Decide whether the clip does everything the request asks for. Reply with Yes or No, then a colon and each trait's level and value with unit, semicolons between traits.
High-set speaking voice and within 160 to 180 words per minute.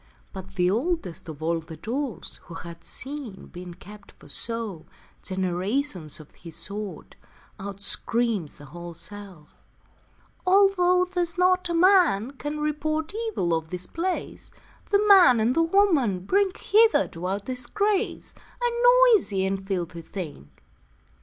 No: high, 225 Hz; average, 140 wpm